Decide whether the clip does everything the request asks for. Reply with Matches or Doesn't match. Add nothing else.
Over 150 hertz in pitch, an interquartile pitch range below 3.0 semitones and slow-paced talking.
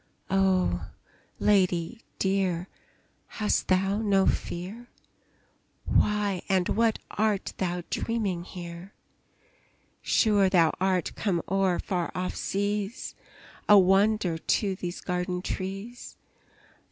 Matches